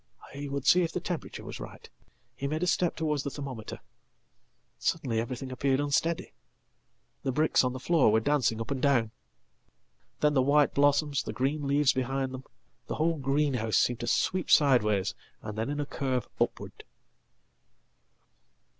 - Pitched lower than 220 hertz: Yes, medium, 140 Hz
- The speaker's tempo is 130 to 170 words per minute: Yes, average, 150 wpm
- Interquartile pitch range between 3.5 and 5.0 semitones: No, average, 2.8 semitones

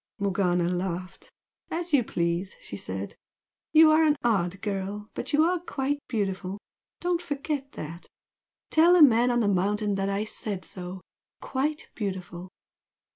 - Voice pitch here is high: Yes, high, 205 Hz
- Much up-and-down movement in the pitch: Yes, wide, 7.7 semitones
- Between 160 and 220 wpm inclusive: No, average, 145 wpm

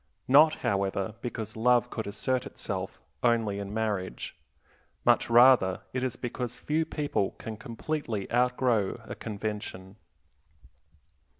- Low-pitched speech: Yes, low, 115 Hz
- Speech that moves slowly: Yes, slow, 115 wpm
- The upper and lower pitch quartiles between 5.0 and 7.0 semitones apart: No, average, 3.8 semitones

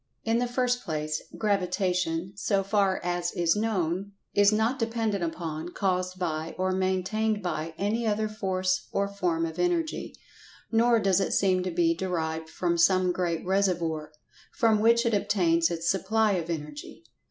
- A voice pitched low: No, medium, 185 Hz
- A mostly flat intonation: No, average, 4.0 semitones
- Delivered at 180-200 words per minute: No, average, 155 wpm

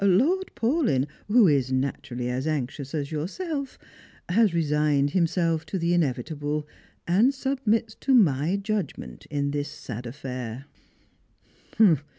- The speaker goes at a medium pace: No, slow, 120 wpm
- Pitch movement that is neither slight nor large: No, wide, 7.0 semitones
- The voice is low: No, medium, 155 Hz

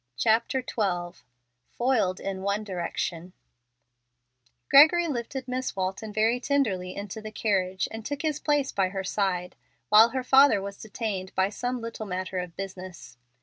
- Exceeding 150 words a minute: No, average, 145 wpm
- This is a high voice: Yes, high, 210 Hz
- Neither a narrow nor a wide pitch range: Yes, average, 4.8 semitones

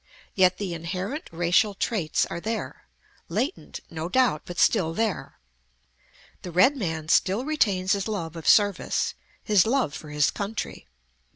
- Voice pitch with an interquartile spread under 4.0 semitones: No, average, 4.6 semitones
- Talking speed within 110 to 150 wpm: Yes, average, 145 wpm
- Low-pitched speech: No, high, 190 Hz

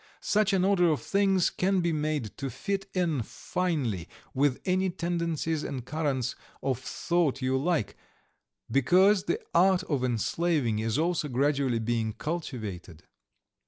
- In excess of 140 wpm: No, slow, 135 wpm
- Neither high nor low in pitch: Yes, medium, 155 Hz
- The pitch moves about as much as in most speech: No, wide, 5.9 semitones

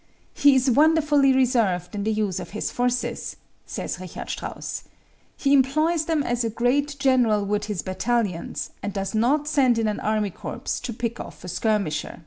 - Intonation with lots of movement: No, average, 4.8 semitones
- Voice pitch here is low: No, high, 235 Hz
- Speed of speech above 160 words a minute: Yes, average, 175 wpm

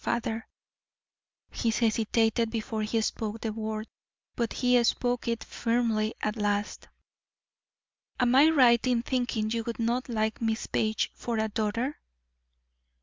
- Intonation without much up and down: Yes, narrow, 1.7 semitones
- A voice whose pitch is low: No, high, 230 Hz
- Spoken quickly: No, slow, 135 wpm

